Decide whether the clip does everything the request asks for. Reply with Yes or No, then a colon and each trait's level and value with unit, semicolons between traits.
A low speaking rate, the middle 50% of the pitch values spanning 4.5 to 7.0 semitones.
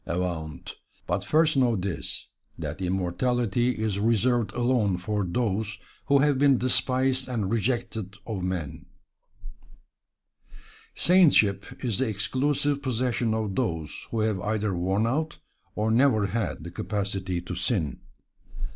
Yes: slow, 125 wpm; average, 4.9 semitones